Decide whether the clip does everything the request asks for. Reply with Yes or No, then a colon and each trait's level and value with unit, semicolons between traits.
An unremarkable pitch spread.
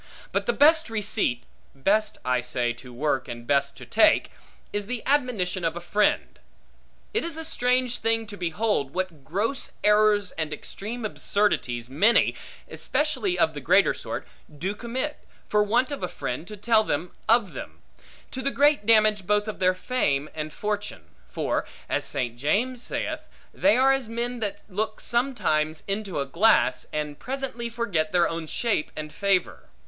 No: wide, 7.2 semitones